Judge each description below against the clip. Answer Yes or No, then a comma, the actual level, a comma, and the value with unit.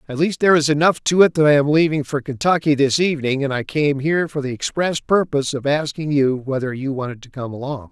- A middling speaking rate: No, fast, 245 wpm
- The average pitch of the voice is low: No, medium, 145 Hz